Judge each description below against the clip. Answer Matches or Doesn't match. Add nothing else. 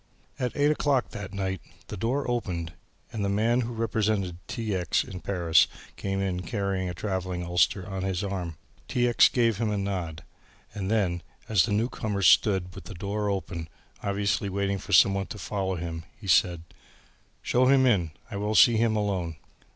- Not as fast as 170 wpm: Doesn't match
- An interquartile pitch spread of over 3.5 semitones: Doesn't match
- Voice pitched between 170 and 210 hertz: Doesn't match